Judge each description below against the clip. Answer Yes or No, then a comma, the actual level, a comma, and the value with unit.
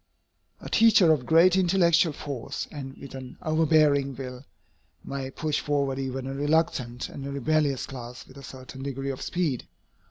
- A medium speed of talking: Yes, average, 160 wpm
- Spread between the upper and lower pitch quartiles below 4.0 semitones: Yes, average, 2.9 semitones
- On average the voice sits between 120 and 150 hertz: Yes, medium, 140 Hz